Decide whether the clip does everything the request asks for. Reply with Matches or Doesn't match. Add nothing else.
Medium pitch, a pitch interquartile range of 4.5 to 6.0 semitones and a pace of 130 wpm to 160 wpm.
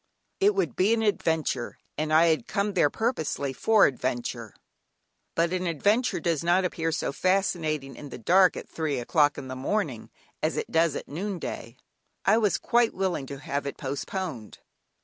Doesn't match